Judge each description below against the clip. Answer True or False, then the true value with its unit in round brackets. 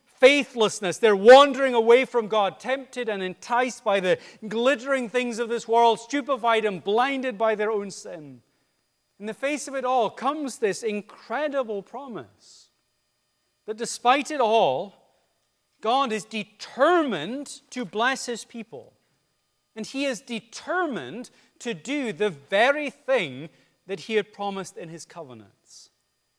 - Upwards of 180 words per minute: False (135 wpm)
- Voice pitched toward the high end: True (230 Hz)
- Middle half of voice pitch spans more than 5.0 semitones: False (4.5 semitones)